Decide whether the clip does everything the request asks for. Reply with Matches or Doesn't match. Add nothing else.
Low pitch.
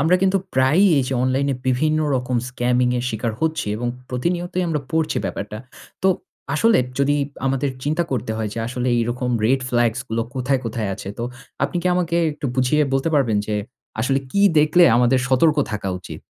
Matches